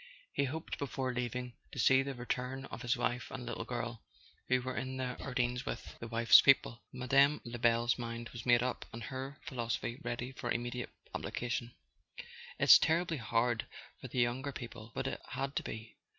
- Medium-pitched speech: No, low, 125 Hz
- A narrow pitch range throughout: Yes, narrow, 1.8 semitones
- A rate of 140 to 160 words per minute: No, average, 180 wpm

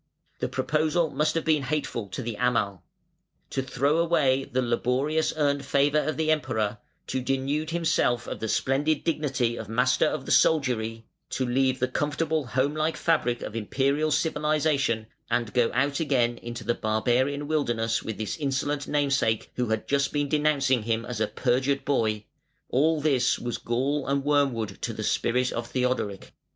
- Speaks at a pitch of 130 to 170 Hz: Yes, low, 135 Hz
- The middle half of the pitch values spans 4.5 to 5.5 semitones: No, average, 3.8 semitones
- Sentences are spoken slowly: No, average, 165 wpm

